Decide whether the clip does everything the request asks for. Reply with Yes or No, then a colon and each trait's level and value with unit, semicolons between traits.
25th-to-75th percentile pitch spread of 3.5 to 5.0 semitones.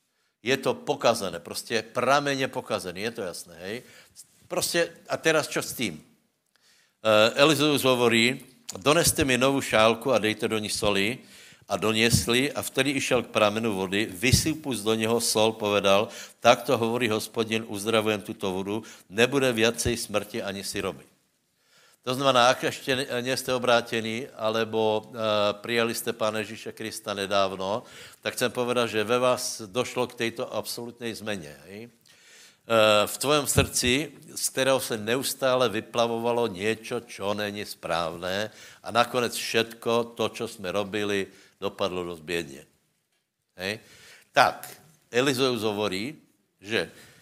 No: average, 2.7 semitones